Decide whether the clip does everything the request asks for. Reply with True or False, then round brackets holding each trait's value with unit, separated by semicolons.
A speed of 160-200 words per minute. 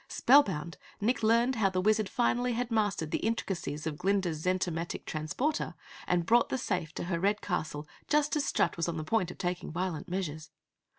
True (185 wpm)